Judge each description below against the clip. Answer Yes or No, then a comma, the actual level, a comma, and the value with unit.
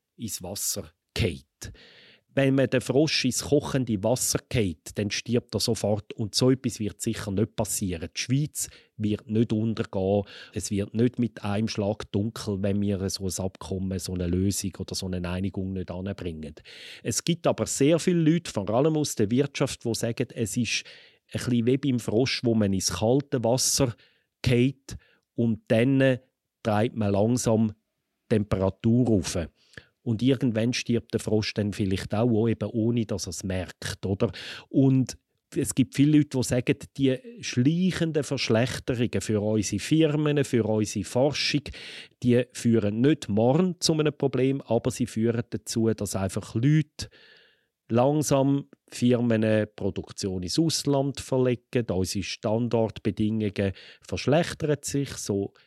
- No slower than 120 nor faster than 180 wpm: Yes, average, 150 wpm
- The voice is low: Yes, low, 115 Hz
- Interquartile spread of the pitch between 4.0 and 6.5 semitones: Yes, average, 4.3 semitones